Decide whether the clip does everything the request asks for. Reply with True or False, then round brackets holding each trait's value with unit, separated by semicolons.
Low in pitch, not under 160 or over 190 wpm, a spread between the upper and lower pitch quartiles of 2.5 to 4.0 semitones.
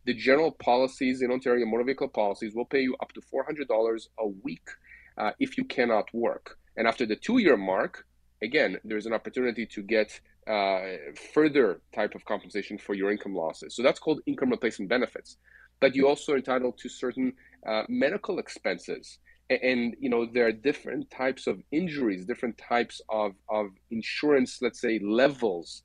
True (120 Hz; 170 wpm; 3.3 semitones)